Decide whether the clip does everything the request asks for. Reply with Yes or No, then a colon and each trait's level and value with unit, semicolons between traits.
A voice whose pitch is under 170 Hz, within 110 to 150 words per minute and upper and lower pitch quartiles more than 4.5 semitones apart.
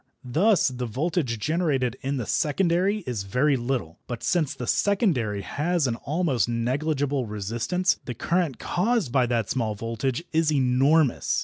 Yes: low, 135 Hz; average, 145 wpm; wide, 5.6 semitones